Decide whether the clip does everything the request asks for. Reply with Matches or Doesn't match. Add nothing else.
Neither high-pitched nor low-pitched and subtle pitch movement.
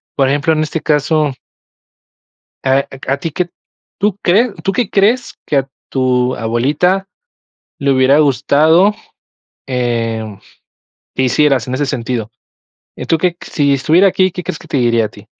Doesn't match